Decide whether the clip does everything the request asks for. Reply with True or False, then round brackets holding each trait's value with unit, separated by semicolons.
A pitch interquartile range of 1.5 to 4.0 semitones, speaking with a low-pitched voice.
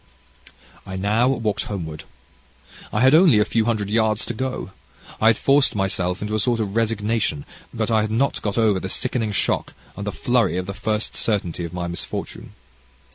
True (2.9 semitones; 110 Hz)